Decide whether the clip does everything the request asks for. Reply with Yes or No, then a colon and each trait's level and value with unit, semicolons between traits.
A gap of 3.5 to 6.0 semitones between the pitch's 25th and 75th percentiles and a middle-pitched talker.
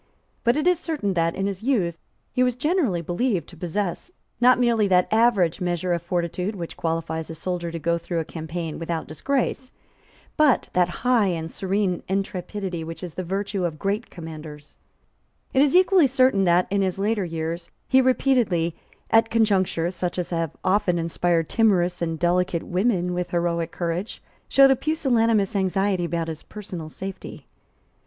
Yes: average, 4.8 semitones; medium, 180 Hz